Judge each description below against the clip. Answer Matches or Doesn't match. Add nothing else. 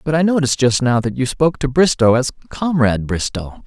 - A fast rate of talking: Matches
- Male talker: Matches